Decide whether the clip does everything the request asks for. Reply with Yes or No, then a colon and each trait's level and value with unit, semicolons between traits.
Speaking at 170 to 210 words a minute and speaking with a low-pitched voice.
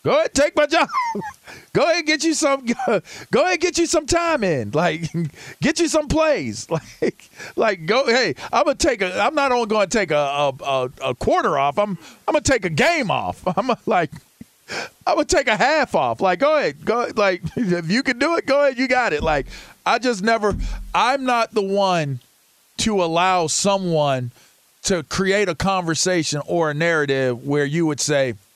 No: average, 195 wpm; high, 200 Hz